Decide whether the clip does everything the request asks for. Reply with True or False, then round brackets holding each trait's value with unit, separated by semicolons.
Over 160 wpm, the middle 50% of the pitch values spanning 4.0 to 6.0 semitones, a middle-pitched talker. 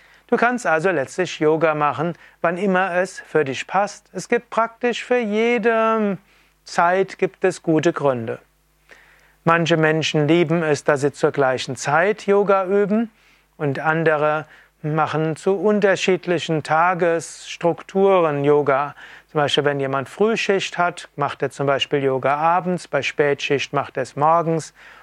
False (140 wpm; 4.5 semitones; 165 Hz)